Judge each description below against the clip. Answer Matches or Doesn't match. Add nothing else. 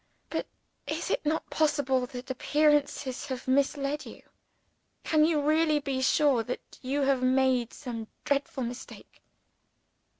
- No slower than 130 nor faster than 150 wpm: Matches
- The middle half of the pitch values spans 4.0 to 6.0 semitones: Doesn't match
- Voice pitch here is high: Matches